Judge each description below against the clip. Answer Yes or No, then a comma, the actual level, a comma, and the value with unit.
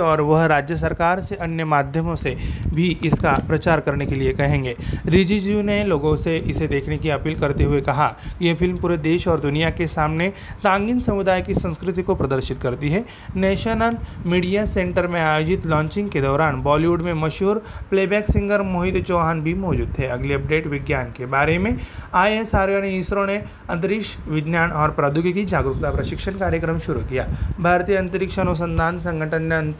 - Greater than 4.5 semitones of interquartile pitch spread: No, average, 3.8 semitones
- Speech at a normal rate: No, fast, 175 wpm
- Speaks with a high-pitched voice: No, medium, 165 Hz